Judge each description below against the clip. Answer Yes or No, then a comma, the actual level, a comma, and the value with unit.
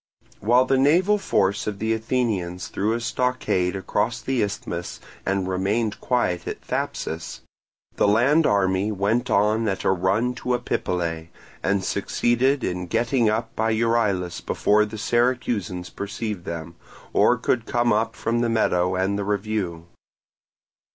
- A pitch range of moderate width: Yes, average, 4.0 semitones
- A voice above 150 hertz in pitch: No, low, 105 Hz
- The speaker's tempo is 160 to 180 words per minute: No, average, 145 wpm